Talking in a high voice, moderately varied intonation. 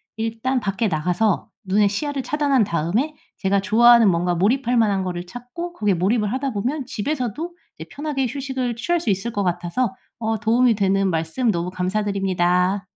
Yes: high, 215 Hz; average, 5.0 semitones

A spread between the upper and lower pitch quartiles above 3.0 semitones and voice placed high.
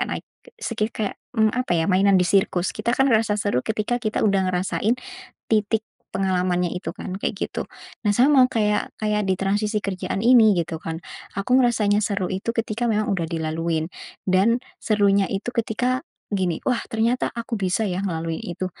Yes: average, 3.4 semitones; high, 205 Hz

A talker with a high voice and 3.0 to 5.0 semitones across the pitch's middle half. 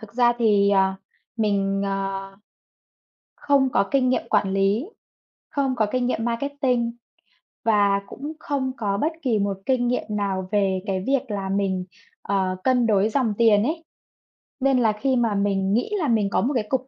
Yes: high, 215 Hz; average, 4.3 semitones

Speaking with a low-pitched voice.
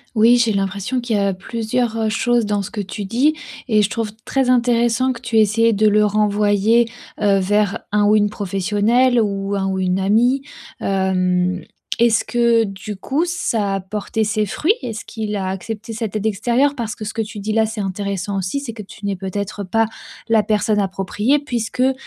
No: high, 215 Hz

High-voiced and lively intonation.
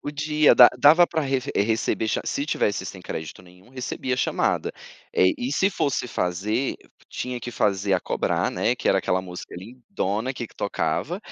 No: low, 120 Hz; wide, 6.1 semitones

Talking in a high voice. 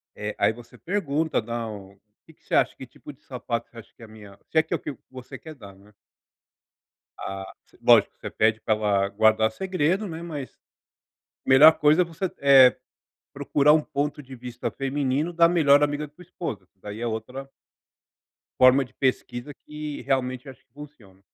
No: low, 130 Hz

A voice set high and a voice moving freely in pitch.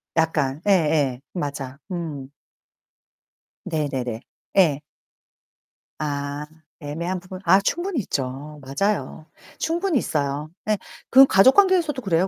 No: medium, 160 Hz; wide, 5.7 semitones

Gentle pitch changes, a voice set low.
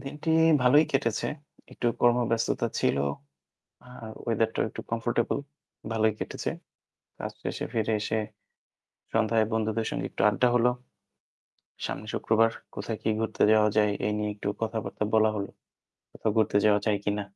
Yes: narrow, 1.5 semitones; low, 110 Hz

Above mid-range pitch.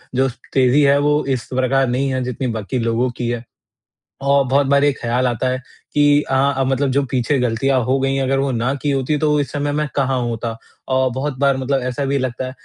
No: low, 135 Hz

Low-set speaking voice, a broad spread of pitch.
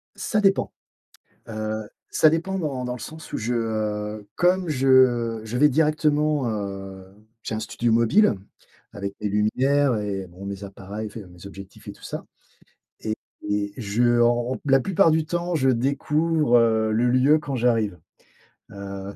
Yes: low, 120 Hz; wide, 5.8 semitones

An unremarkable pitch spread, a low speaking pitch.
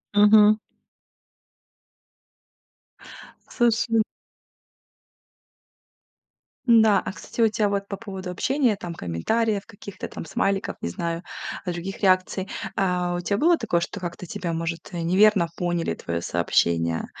No: average, 3.8 semitones; high, 190 Hz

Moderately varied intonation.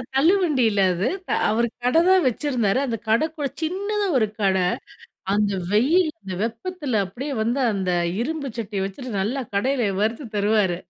No: wide, 6.4 semitones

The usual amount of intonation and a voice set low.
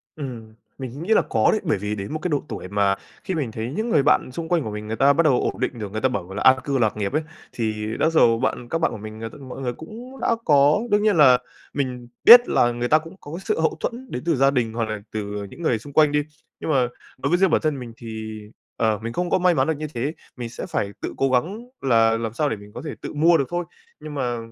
No: wide, 6.0 semitones; low, 130 Hz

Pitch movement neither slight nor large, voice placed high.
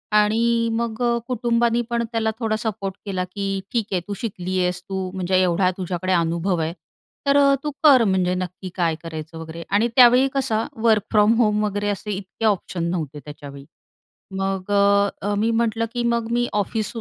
Yes: average, 4.0 semitones; high, 205 Hz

